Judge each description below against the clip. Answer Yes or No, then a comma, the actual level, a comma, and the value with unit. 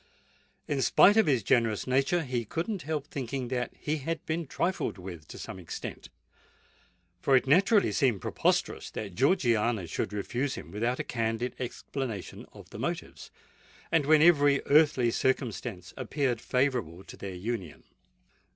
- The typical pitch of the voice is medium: No, low, 130 Hz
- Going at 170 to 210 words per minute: No, average, 150 wpm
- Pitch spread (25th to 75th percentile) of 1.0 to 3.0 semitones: No, average, 4.5 semitones